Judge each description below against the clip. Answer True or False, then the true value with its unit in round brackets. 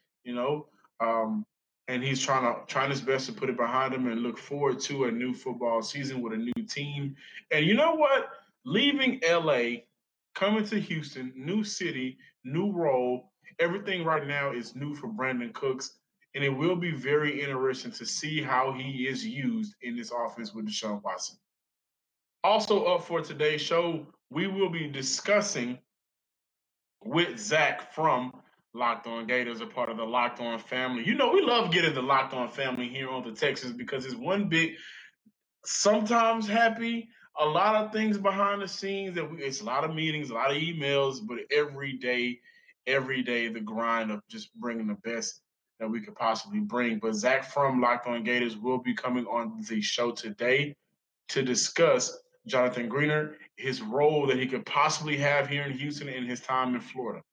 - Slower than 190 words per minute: True (180 wpm)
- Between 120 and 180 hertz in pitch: True (135 Hz)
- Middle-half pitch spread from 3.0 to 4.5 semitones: False (5.6 semitones)